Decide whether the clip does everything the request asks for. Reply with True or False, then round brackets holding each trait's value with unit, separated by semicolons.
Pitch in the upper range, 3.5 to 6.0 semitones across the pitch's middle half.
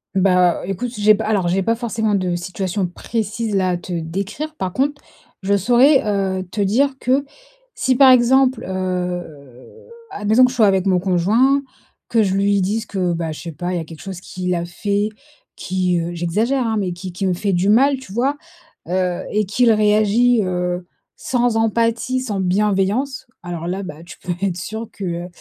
True (200 Hz; 4.3 semitones)